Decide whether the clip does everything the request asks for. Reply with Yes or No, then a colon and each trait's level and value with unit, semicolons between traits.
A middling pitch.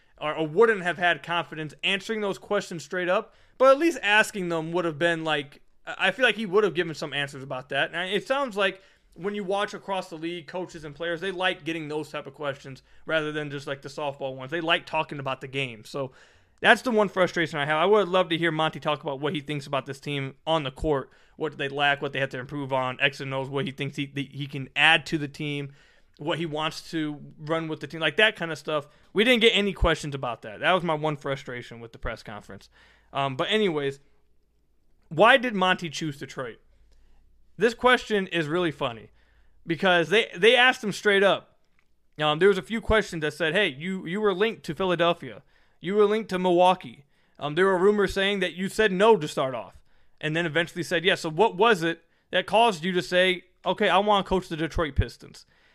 Yes: medium, 165 Hz